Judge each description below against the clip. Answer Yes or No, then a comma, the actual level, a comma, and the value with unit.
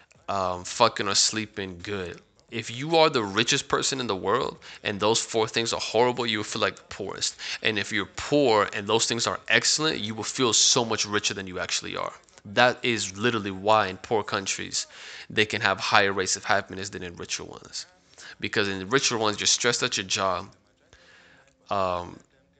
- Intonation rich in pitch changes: No, average, 3.5 semitones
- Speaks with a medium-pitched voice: No, low, 110 Hz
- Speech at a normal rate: Yes, average, 195 wpm